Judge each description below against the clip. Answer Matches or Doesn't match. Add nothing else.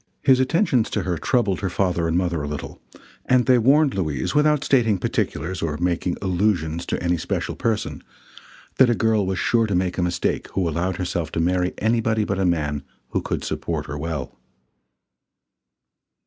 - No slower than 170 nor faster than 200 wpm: Matches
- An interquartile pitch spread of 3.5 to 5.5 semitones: Matches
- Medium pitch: Doesn't match